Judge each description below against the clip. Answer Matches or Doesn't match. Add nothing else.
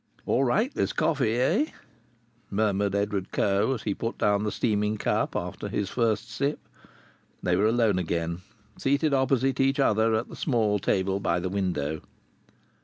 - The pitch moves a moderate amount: Matches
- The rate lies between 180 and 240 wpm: Doesn't match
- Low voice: Matches